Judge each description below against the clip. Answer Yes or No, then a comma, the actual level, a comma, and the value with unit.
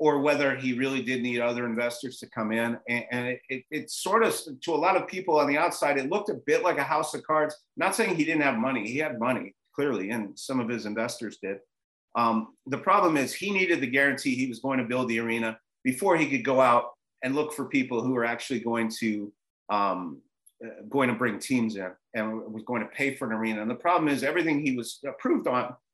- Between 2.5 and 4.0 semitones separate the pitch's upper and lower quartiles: Yes, average, 3.5 semitones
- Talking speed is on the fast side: Yes, fast, 240 wpm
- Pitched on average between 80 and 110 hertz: No, low, 125 Hz